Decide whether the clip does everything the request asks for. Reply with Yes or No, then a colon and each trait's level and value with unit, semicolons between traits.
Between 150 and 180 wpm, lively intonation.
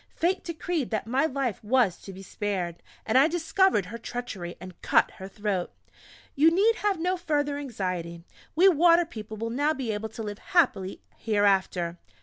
Yes: average, 170 wpm; wide, 8.4 semitones